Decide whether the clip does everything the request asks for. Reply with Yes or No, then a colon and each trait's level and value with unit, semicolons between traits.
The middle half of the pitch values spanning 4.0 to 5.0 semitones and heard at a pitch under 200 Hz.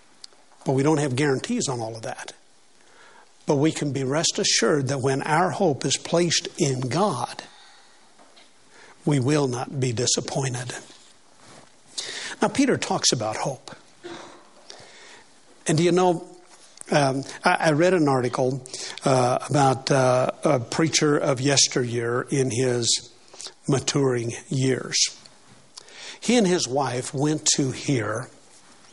Yes: average, 4.6 semitones; medium, 140 Hz